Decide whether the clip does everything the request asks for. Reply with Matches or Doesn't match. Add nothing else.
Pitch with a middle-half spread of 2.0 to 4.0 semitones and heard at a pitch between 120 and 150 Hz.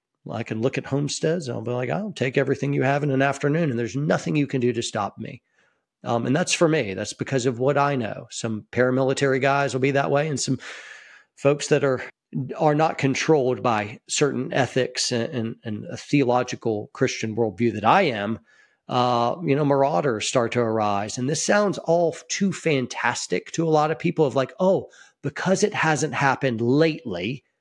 Matches